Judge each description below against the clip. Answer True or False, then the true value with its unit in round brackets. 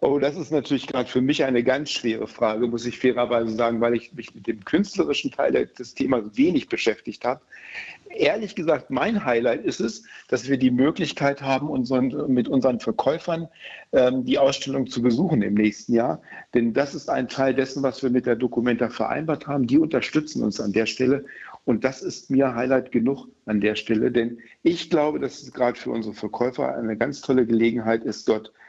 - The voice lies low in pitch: True (130 Hz)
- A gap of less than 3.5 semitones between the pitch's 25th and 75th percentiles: True (3.1 semitones)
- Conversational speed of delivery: False (195 wpm)